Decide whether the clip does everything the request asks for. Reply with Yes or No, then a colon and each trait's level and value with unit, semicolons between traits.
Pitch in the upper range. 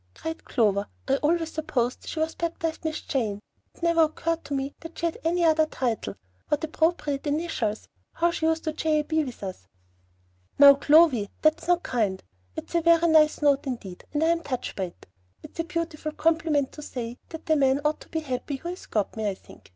Yes: very high, 305 Hz